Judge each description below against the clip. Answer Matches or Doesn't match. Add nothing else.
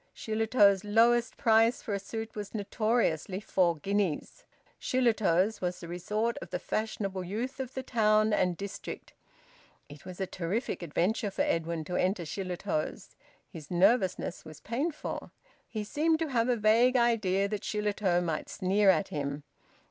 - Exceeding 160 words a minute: Doesn't match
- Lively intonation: Doesn't match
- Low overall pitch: Doesn't match